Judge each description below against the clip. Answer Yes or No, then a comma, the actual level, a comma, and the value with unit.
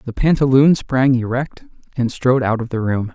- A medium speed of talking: Yes, average, 190 wpm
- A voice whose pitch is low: Yes, low, 125 Hz